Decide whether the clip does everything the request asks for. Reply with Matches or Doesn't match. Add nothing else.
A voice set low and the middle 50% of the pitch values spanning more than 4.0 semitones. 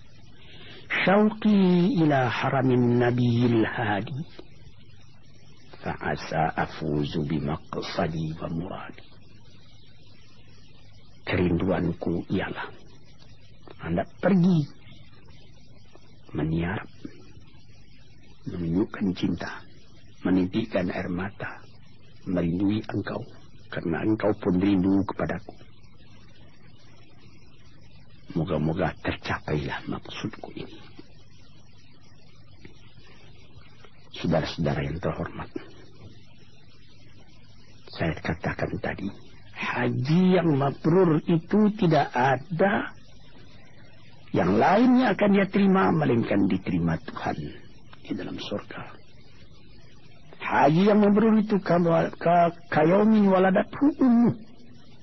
Matches